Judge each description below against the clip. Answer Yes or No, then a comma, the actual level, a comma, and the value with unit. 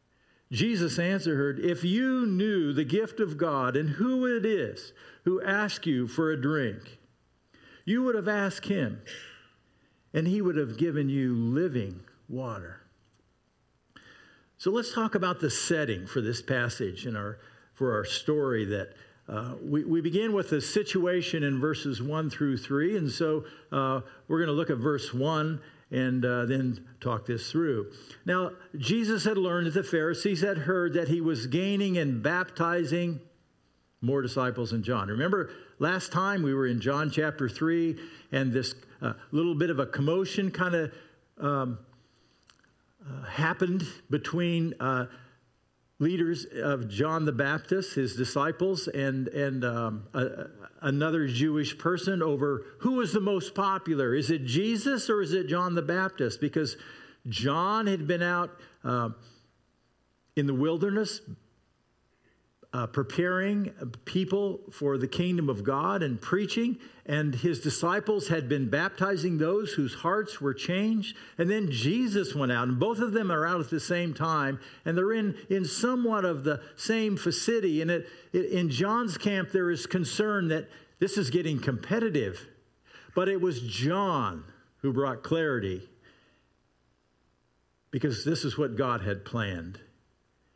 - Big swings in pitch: Yes, wide, 5.8 semitones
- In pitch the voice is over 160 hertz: No, medium, 155 Hz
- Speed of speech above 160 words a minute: No, average, 150 wpm